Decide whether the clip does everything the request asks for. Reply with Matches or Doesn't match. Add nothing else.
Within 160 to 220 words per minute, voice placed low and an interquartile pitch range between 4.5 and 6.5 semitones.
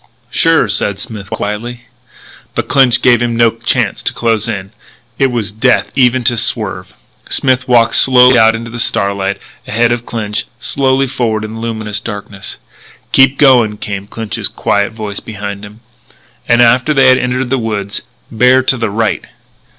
Doesn't match